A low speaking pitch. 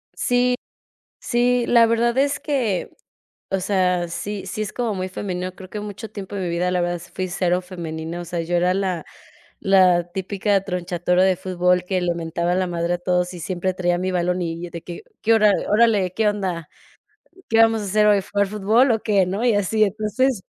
No: medium, 185 Hz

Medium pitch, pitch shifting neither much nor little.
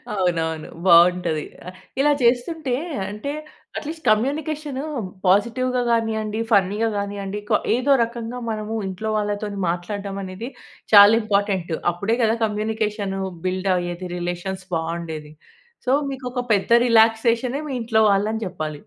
No: high, 210 Hz; average, 4.0 semitones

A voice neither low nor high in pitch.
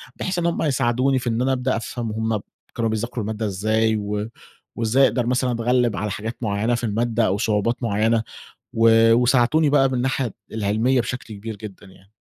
No: low, 115 Hz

